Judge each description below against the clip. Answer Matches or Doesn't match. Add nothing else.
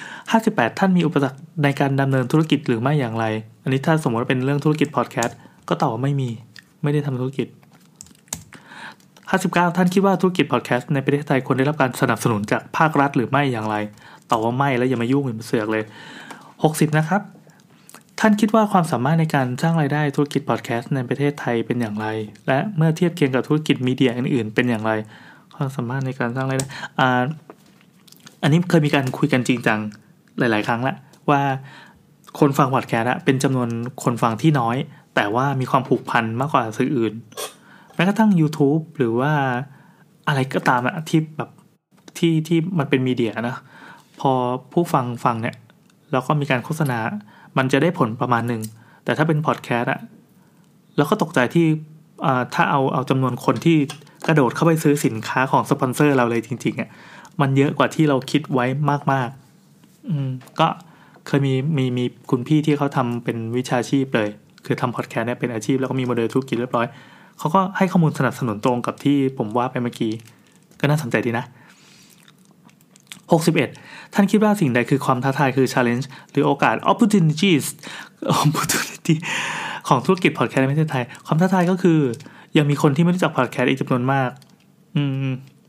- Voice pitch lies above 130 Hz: Matches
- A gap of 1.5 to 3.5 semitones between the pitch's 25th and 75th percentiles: Doesn't match